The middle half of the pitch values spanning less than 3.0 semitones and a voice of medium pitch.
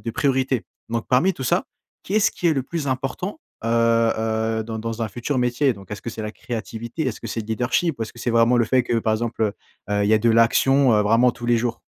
No: narrow, 2.5 semitones; low, 115 Hz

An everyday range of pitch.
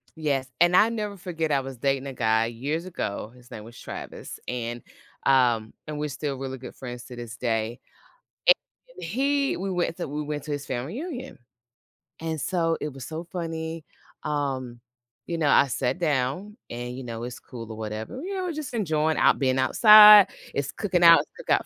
No: wide, 6.0 semitones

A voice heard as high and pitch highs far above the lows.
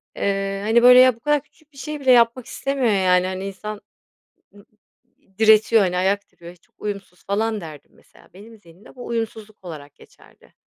No: high, 210 Hz; average, 3.9 semitones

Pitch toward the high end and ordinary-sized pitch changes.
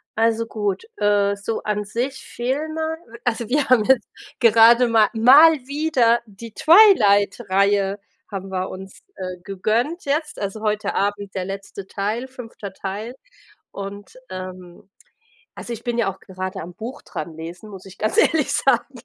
Yes: high, 215 Hz; average, 4.0 semitones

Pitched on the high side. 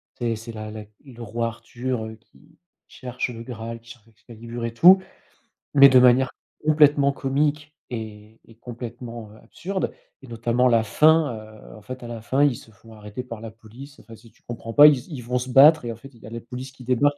No: low, 120 Hz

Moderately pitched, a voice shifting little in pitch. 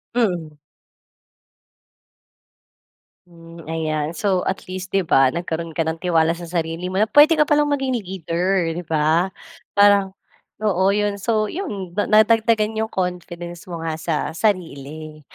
No: medium, 180 Hz; average, 4.1 semitones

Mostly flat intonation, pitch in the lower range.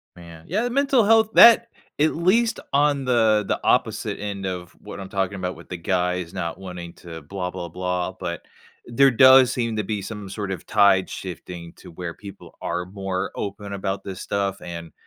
No: average, 4.7 semitones; very low, 95 Hz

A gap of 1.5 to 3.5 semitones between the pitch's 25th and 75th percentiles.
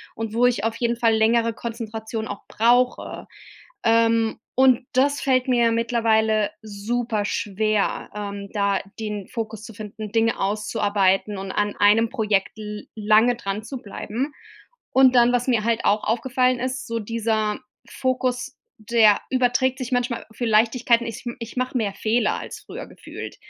Yes: narrow, 2.4 semitones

